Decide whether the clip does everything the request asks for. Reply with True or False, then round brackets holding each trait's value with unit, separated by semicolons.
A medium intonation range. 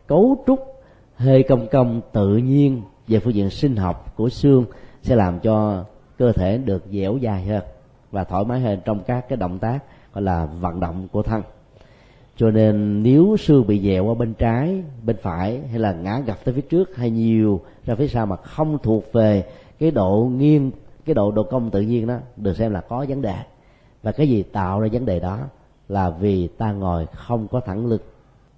True (4.5 semitones)